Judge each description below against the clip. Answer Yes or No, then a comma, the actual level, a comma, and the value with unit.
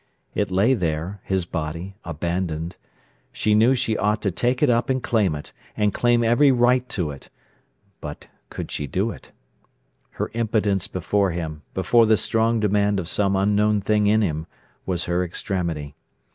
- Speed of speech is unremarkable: Yes, average, 160 wpm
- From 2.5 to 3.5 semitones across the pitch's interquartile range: No, average, 4.4 semitones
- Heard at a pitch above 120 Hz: No, low, 100 Hz